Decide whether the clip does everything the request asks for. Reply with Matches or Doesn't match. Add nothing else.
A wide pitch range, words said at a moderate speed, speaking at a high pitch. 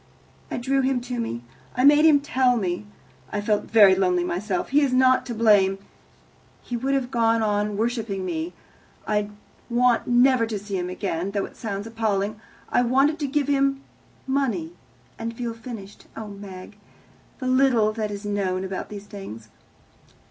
Doesn't match